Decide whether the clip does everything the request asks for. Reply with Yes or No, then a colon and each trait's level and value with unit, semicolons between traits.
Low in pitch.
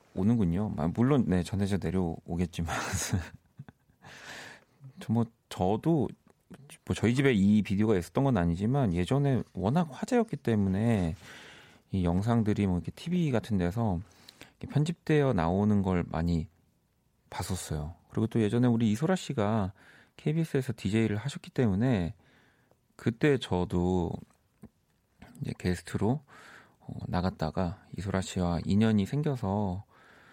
Yes: low, 105 Hz